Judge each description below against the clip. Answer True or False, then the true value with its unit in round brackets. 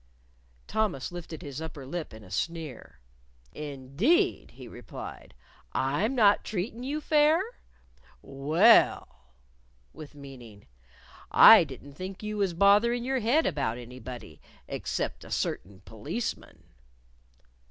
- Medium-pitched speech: True (165 Hz)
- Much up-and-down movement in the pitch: True (8.5 semitones)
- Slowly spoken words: True (110 wpm)